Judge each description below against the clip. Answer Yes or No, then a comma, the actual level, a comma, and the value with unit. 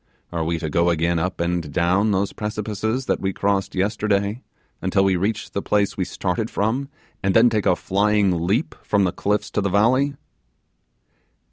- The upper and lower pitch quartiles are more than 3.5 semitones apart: No, average, 3.0 semitones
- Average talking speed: Yes, average, 175 wpm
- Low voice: Yes, low, 100 Hz